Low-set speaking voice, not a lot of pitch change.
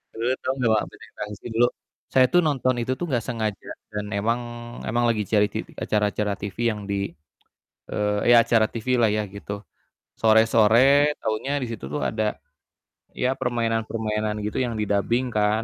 Yes: low, 110 Hz; narrow, 2.3 semitones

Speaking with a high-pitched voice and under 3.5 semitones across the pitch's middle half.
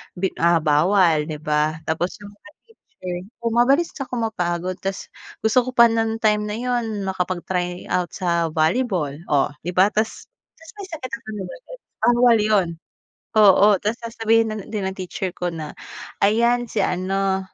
No: high, 195 Hz; average, 4.3 semitones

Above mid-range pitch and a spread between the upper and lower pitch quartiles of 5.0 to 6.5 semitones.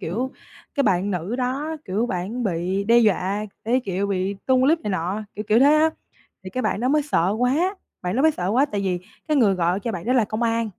Yes: high, 215 Hz; average, 5.3 semitones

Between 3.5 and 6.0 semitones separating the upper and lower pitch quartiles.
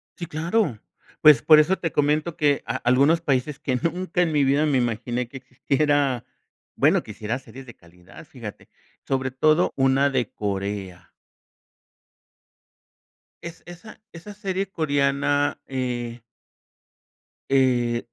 Yes: average, 4.2 semitones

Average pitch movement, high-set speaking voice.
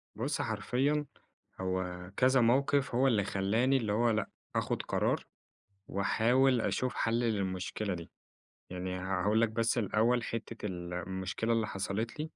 No: average, 4.0 semitones; low, 110 Hz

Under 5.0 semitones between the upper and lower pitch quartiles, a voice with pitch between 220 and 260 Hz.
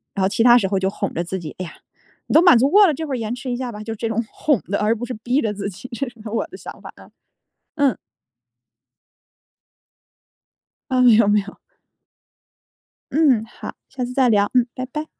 Yes: average, 3.8 semitones; high, 235 Hz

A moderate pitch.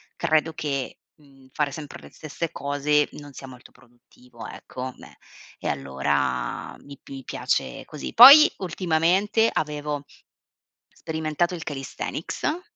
Yes: medium, 150 Hz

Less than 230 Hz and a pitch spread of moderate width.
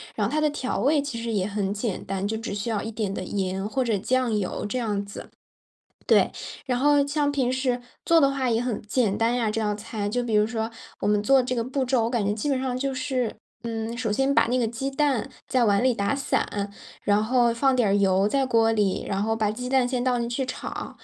No: high, 235 Hz; average, 3.7 semitones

